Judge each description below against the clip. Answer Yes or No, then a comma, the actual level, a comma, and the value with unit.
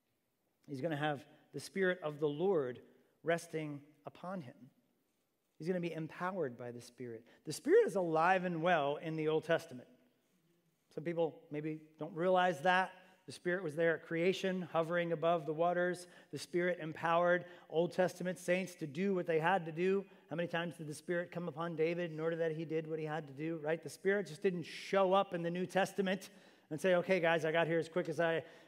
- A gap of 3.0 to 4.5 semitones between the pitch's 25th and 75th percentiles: No, narrow, 2.4 semitones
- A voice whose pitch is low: No, medium, 170 Hz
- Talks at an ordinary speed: No, fast, 210 wpm